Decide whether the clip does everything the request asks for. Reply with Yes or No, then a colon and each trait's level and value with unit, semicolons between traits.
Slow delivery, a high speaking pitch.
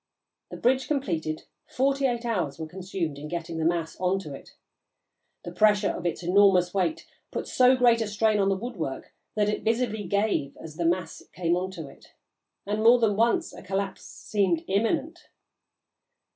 No: average, 175 wpm; high, 195 Hz